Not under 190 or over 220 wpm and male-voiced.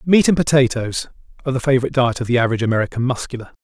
Yes: average, 200 wpm; male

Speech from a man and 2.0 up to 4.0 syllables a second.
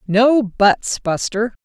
No: female; 2.8 syllables/s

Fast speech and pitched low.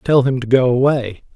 Yes: fast, 220 wpm; low, 130 Hz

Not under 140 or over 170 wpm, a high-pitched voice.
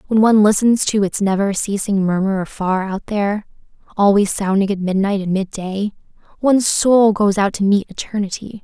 Yes: average, 165 wpm; high, 200 Hz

